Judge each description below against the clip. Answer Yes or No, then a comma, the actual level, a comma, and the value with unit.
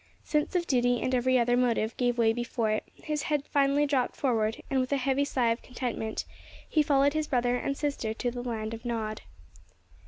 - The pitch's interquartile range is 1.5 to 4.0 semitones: Yes, average, 3.1 semitones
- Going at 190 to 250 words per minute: Yes, average, 200 wpm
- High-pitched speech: Yes, very high, 250 Hz